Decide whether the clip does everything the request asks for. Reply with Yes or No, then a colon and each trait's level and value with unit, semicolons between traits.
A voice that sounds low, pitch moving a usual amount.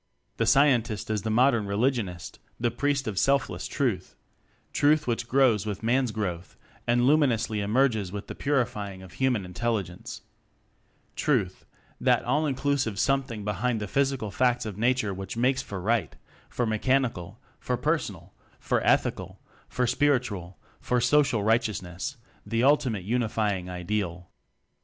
Yes: low, 115 Hz; average, 4.6 semitones